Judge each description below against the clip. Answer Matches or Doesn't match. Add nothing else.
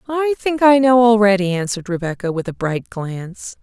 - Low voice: Doesn't match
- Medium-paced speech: Matches